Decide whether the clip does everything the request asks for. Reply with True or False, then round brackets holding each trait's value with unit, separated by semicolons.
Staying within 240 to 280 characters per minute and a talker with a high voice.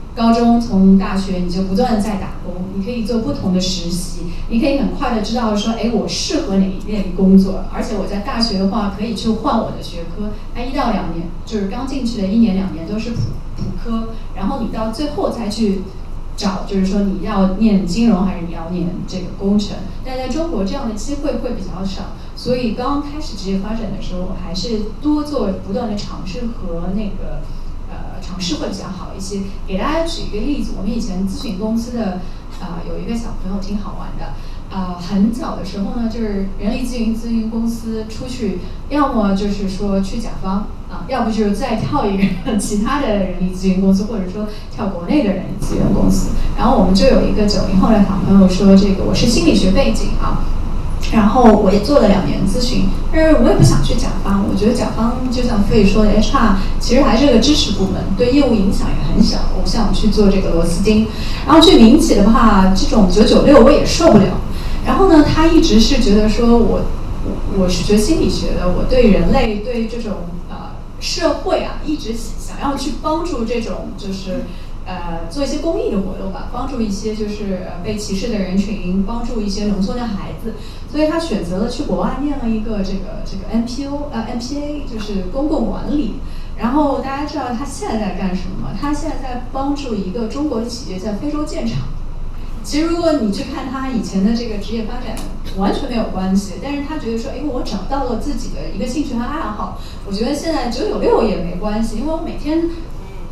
False (310 characters per minute; 220 Hz)